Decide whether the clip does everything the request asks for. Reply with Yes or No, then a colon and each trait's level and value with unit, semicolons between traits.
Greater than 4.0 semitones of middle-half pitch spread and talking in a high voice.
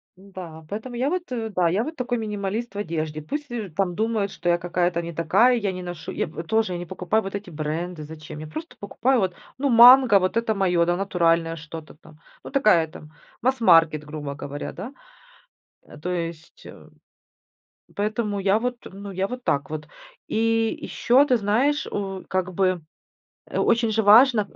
Yes: average, 5.2 semitones; high, 195 Hz